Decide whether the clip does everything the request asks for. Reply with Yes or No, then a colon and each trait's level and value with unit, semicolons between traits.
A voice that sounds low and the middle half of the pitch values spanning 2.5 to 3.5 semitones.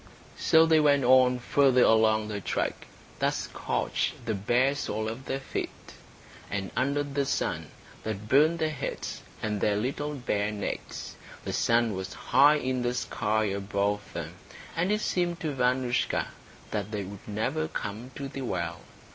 No: low, 125 Hz; average, 5.1 semitones